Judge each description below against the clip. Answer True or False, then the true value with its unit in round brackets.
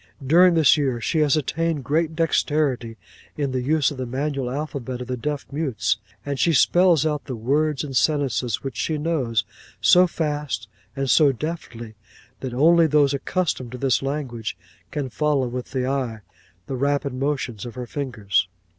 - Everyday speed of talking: True (170 wpm)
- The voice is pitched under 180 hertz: True (140 Hz)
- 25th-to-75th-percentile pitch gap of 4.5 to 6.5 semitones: False (3.4 semitones)